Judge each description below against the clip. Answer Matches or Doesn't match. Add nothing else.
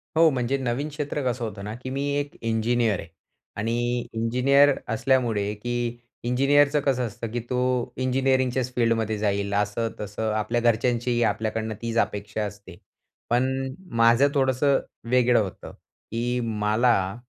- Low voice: Matches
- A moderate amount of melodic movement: Matches